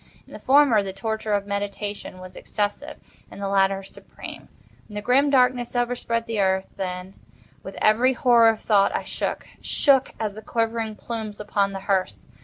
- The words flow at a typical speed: Yes, average, 165 wpm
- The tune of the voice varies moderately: Yes, average, 3.1 semitones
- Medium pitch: No, high, 215 Hz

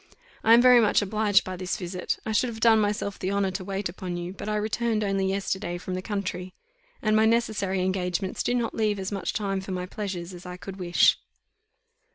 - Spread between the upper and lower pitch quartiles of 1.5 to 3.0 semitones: Yes, narrow, 2.6 semitones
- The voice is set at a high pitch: Yes, high, 195 Hz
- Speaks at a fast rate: Yes, fast, 215 wpm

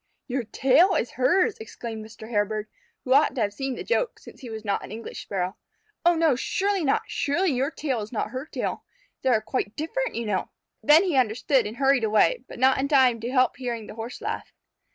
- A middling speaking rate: No, fast, 215 wpm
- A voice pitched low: No, very high, 255 Hz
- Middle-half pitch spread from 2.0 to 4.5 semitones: No, average, 5.1 semitones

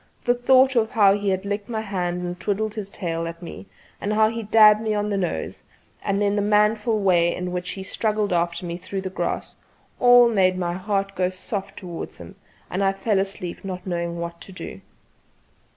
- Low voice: No, high, 195 Hz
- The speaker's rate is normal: No, fast, 210 wpm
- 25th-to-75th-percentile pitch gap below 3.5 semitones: Yes, average, 2.8 semitones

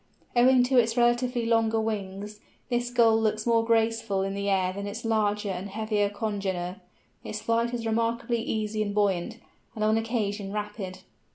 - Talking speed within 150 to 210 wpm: Yes, average, 165 wpm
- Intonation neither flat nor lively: No, narrow, 2.2 semitones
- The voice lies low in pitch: No, high, 215 Hz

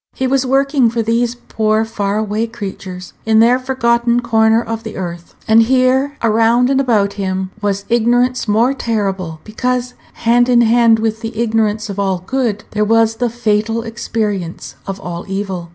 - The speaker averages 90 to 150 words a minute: No, average, 165 wpm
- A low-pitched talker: No, high, 225 Hz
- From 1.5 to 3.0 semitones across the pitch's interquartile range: Yes, average, 2.7 semitones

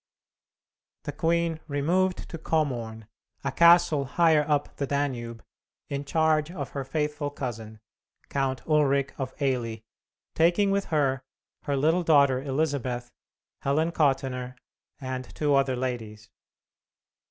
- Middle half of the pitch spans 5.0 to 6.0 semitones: No, average, 3.5 semitones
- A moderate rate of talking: No, slow, 120 wpm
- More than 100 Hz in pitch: Yes, medium, 140 Hz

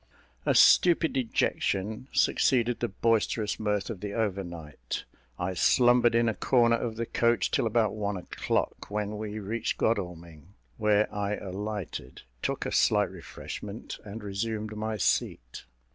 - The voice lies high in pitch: No, low, 105 Hz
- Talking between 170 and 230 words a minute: No, average, 140 wpm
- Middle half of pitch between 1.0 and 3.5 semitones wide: Yes, average, 2.7 semitones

